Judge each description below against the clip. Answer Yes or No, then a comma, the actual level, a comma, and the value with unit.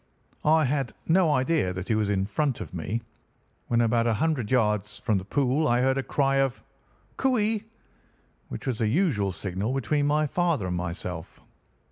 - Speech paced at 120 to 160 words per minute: No, average, 175 wpm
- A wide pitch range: Yes, wide, 6.3 semitones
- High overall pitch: No, low, 125 Hz